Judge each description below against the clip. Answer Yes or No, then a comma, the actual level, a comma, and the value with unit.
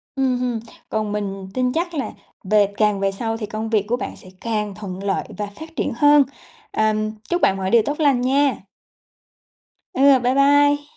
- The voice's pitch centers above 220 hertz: Yes, high, 230 Hz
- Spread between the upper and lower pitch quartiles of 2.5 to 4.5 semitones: No, average, 5.0 semitones